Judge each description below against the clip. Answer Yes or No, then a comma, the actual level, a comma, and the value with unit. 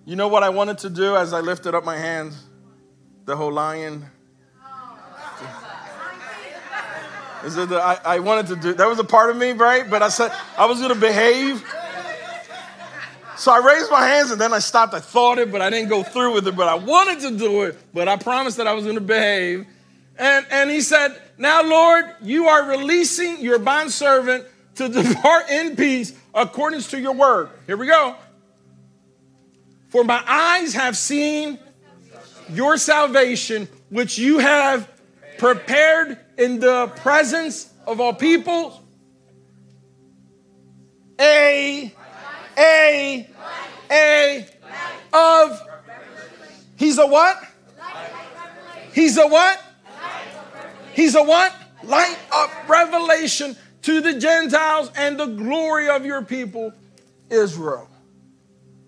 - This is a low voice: No, very high, 250 Hz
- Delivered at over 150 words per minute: No, average, 140 wpm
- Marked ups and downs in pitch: Yes, wide, 8.2 semitones